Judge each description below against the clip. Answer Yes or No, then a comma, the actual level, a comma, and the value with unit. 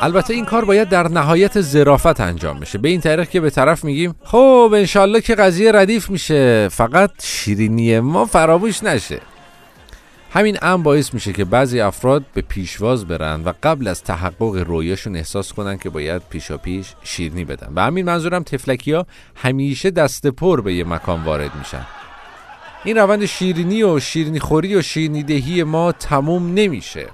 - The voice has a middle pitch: Yes, medium, 145 Hz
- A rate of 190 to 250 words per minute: No, average, 165 wpm